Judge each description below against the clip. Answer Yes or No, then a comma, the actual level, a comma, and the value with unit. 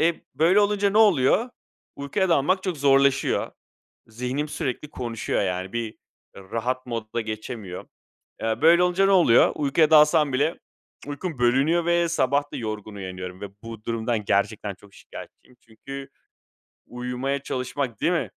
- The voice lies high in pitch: No, low, 130 Hz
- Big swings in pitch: Yes, wide, 5.9 semitones